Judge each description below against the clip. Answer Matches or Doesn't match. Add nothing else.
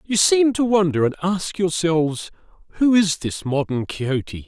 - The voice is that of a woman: Doesn't match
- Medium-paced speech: Matches